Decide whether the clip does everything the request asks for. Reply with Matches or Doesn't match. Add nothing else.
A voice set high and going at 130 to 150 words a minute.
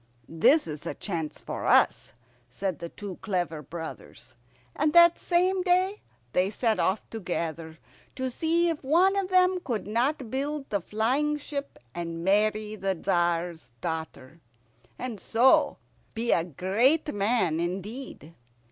Matches